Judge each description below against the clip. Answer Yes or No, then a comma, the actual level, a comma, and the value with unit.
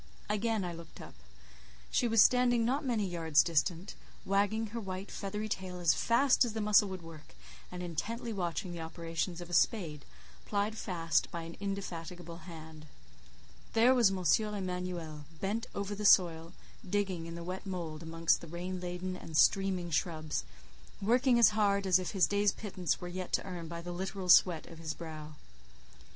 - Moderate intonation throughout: Yes, average, 3.6 semitones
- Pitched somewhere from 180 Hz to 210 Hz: Yes, medium, 185 Hz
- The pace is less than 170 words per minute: No, average, 175 wpm